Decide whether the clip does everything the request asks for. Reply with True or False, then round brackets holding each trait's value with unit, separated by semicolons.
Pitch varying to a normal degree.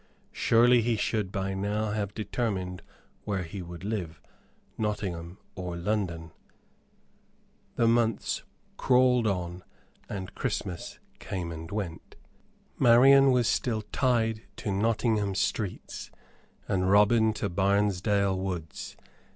True (3.4 semitones)